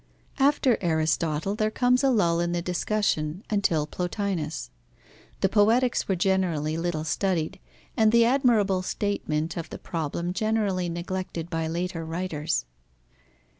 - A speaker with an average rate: No, slow, 130 wpm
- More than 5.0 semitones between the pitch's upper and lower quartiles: No, average, 4.3 semitones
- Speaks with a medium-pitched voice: Yes, medium, 180 Hz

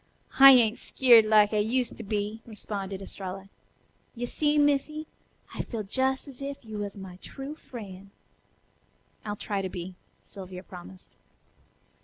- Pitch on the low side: No, high, 215 Hz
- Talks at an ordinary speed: Yes, average, 145 wpm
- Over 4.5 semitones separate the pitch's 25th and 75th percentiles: Yes, average, 5.0 semitones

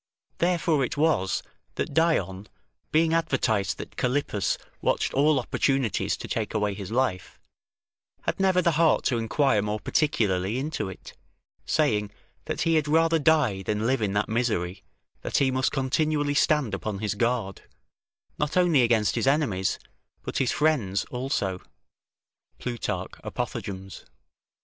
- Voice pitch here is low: Yes, low, 125 Hz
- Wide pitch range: Yes, wide, 6.6 semitones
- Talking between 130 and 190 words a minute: Yes, average, 140 wpm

